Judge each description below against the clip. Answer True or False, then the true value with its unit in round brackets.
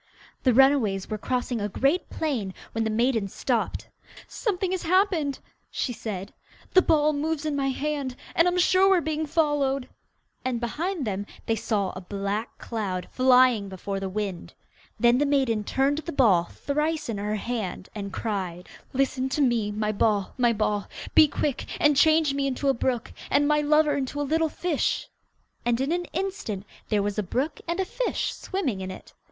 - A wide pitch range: True (6.1 semitones)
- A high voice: True (260 Hz)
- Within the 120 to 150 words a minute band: False (180 wpm)